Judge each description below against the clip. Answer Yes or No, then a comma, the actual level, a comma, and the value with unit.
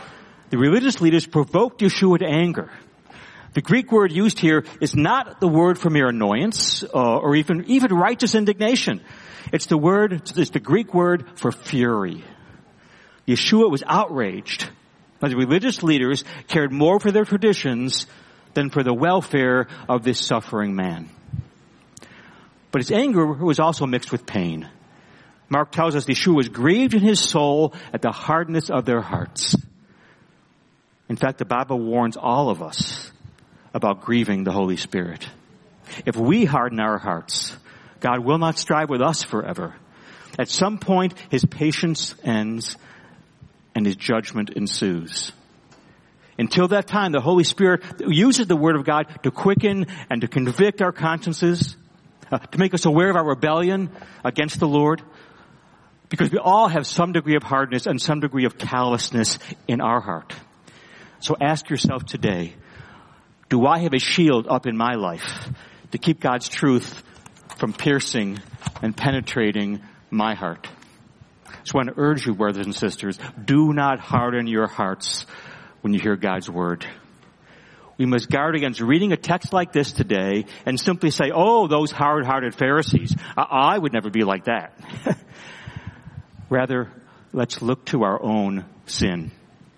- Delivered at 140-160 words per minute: Yes, average, 155 wpm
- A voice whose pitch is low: No, medium, 145 Hz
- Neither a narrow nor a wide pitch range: No, wide, 5.8 semitones